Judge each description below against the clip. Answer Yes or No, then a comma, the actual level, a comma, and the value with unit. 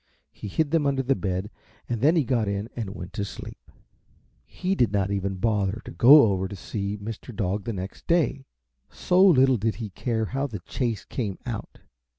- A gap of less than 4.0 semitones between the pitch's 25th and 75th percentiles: No, average, 5.1 semitones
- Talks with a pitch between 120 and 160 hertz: No, low, 110 Hz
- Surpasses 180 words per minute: Yes, average, 195 wpm